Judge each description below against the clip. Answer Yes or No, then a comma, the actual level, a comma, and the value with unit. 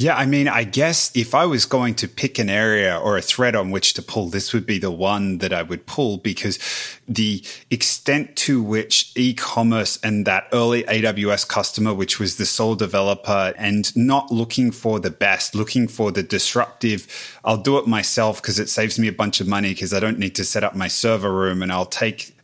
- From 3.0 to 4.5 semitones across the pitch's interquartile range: No, narrow, 2.5 semitones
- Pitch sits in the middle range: No, low, 110 Hz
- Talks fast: Yes, fast, 215 wpm